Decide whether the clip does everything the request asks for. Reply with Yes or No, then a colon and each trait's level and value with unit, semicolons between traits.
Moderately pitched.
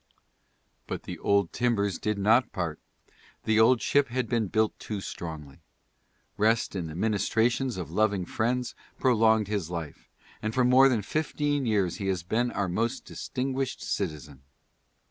No: low, 110 Hz